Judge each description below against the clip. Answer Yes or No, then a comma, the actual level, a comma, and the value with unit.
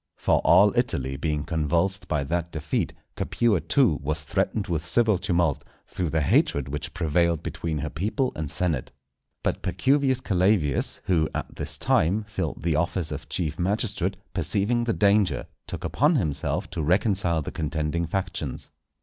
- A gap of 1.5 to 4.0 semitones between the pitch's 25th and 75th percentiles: No, average, 4.5 semitones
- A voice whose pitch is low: Yes, very low, 85 Hz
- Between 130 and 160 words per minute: Yes, average, 155 wpm